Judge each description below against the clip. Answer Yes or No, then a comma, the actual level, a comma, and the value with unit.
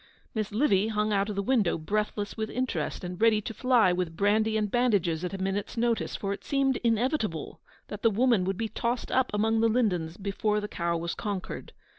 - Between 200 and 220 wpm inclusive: Yes, fast, 205 wpm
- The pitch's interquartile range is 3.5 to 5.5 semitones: No, average, 2.9 semitones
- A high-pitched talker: Yes, high, 210 Hz